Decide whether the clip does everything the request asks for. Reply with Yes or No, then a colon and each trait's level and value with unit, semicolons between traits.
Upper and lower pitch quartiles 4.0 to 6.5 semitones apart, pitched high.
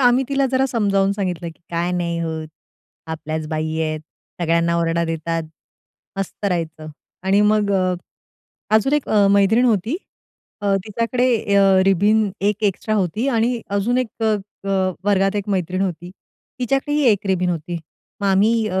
Yes: average, 4.4 semitones; high, 195 Hz